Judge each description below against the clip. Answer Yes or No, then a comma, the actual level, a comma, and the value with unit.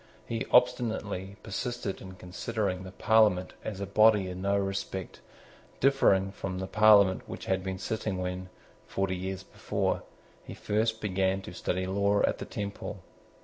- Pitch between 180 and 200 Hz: No, very low, 95 Hz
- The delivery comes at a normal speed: Yes, average, 150 wpm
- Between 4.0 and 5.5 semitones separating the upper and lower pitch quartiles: No, narrow, 2.4 semitones